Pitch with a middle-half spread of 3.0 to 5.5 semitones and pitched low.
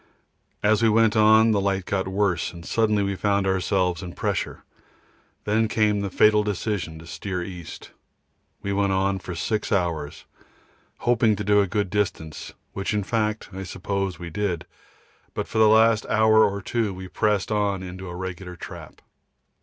No: narrow, 2.5 semitones; low, 100 Hz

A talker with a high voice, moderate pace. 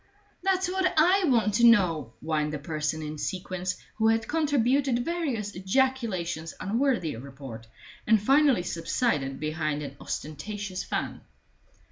No: high, 195 Hz; slow, 130 wpm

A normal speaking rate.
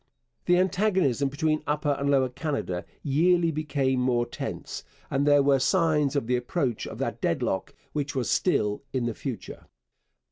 Yes: average, 155 wpm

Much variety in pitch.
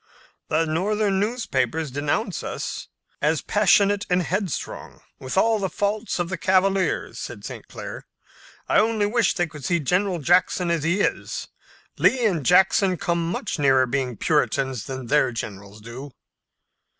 Yes: wide, 5.8 semitones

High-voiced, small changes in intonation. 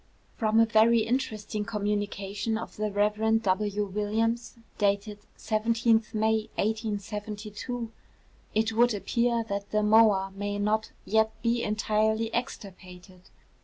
Yes: high, 215 Hz; narrow, 1.5 semitones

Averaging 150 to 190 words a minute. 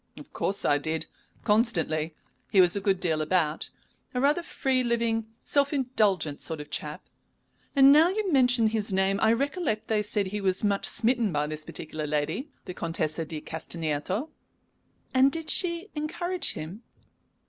Yes: average, 160 wpm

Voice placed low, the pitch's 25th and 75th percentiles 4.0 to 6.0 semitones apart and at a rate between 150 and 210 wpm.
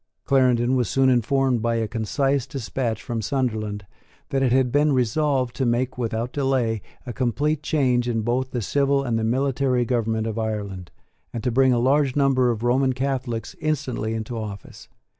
No: low, 125 Hz; average, 3.0 semitones; average, 175 wpm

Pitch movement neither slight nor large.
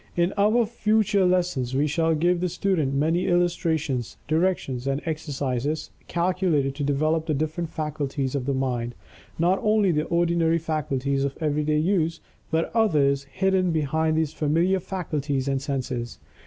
Yes: average, 4.0 semitones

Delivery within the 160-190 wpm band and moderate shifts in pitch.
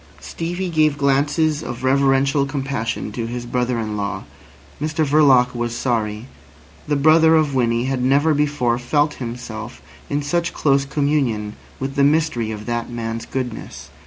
No: average, 150 wpm; average, 3.8 semitones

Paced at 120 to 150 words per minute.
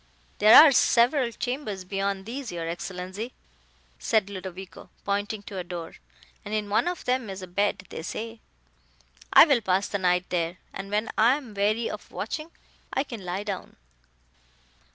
No: average, 165 wpm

